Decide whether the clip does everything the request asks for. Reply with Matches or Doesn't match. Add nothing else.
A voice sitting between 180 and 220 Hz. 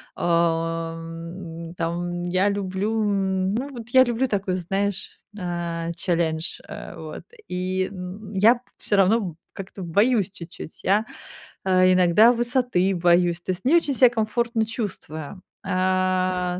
Matches